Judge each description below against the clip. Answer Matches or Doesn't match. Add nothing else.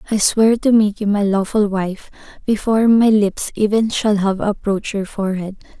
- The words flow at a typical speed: Matches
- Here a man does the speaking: Doesn't match